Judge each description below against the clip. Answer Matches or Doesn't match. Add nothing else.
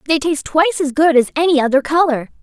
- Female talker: Matches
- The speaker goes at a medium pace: Doesn't match